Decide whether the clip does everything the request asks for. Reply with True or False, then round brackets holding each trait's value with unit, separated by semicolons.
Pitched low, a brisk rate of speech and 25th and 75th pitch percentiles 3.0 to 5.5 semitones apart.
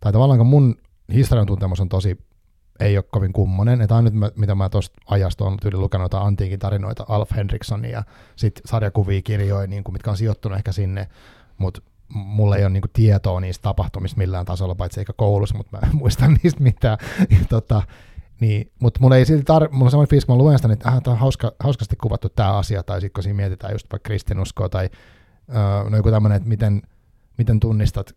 False (105 Hz; 190 wpm; 2.5 semitones)